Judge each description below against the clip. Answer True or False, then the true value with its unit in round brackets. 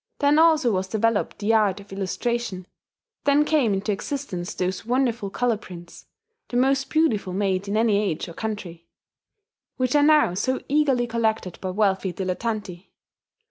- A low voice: False (215 Hz)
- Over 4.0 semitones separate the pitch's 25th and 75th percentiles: True (5.0 semitones)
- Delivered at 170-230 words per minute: False (150 wpm)